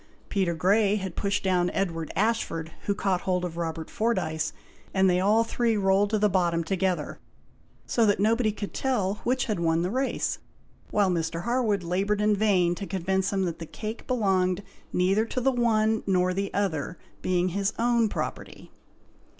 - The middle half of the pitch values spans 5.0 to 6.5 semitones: No, average, 3.2 semitones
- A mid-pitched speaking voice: No, high, 195 Hz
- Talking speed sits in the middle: Yes, average, 175 wpm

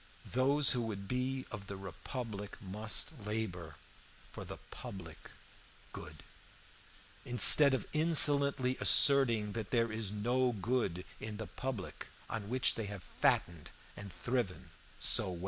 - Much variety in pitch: No, average, 4.5 semitones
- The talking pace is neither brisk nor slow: No, slow, 130 wpm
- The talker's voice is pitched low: Yes, low, 110 Hz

